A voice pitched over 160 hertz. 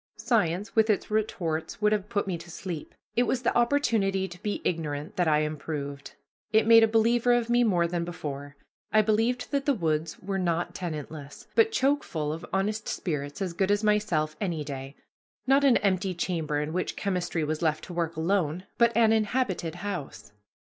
Yes: medium, 185 Hz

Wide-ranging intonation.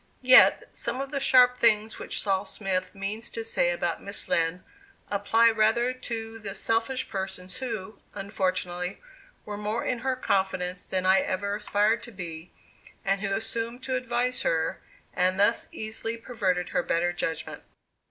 No: average, 3.8 semitones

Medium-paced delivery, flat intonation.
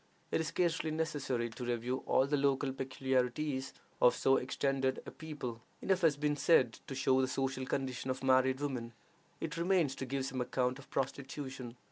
Yes: average, 175 wpm; narrow, 2.1 semitones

